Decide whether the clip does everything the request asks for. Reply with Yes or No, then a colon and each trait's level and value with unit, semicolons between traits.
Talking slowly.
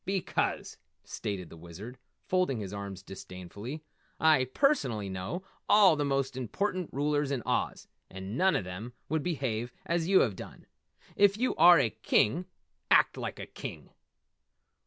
No: average, 150 wpm